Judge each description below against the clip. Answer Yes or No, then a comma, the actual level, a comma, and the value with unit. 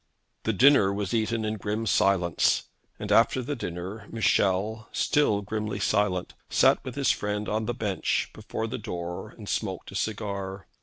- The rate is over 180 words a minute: No, average, 160 wpm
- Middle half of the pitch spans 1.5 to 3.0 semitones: Yes, narrow, 2.4 semitones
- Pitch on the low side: Yes, low, 105 Hz